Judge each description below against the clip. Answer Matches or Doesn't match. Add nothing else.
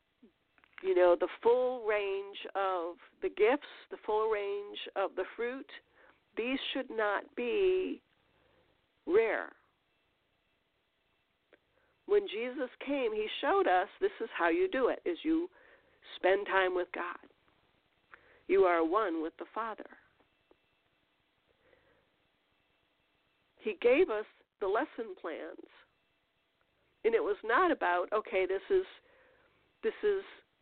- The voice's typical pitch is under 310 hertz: Doesn't match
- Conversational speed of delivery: Doesn't match